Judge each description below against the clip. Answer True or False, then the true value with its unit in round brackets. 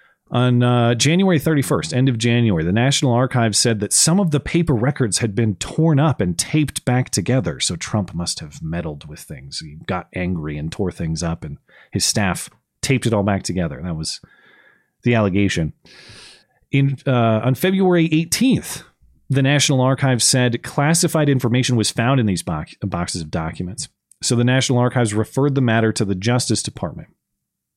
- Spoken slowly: False (175 wpm)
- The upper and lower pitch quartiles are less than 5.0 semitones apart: False (5.4 semitones)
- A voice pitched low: True (120 Hz)